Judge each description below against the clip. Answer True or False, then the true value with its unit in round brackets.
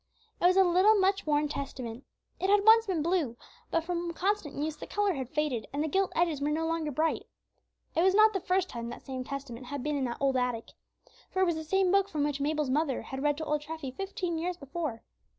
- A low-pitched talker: False (315 Hz)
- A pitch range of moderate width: True (4.8 semitones)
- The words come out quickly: True (240 wpm)